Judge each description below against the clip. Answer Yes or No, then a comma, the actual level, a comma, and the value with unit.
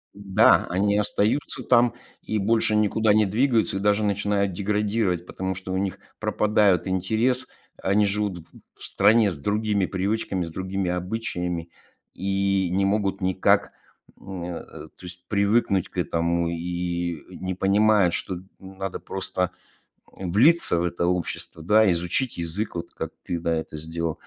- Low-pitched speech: Yes, very low, 95 Hz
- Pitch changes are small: No, average, 3.0 semitones